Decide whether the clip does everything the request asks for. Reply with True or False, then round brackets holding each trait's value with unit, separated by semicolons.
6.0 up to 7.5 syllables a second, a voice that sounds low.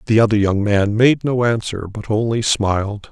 False (4.9 syllables/s; 110 Hz)